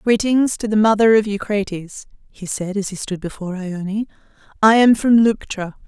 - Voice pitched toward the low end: No, high, 205 Hz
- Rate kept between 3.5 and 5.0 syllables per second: Yes, 4.8 syllables/s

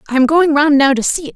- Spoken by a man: No, female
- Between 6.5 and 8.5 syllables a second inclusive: Yes, 7.0 syllables/s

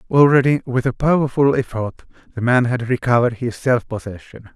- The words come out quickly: No, average, 160 wpm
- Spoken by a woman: No, male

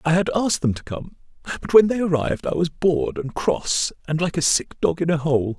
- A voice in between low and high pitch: Yes, medium, 160 Hz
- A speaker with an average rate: No, fast, 245 wpm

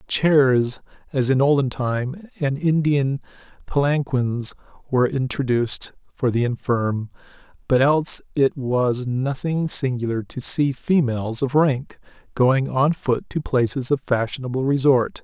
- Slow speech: Yes, slow, 125 wpm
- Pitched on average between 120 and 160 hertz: Yes, low, 135 Hz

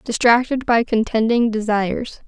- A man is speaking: No, female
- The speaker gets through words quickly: No, slow, 105 wpm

